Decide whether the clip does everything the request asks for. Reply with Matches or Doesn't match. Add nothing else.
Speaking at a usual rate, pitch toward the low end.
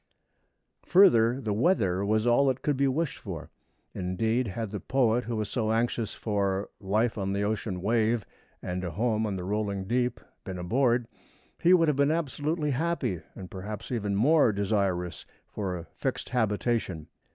Matches